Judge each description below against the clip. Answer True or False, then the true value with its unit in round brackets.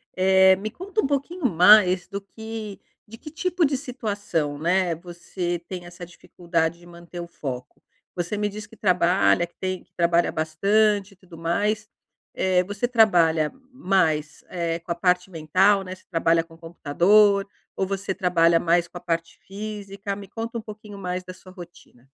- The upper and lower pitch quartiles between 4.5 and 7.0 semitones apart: False (3.3 semitones)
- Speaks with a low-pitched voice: False (185 Hz)